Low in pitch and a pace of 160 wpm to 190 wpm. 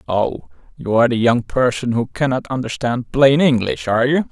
Yes: low, 120 Hz; average, 180 wpm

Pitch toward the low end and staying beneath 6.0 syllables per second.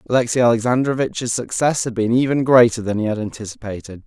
No: low, 115 Hz; 6.2 syllables/s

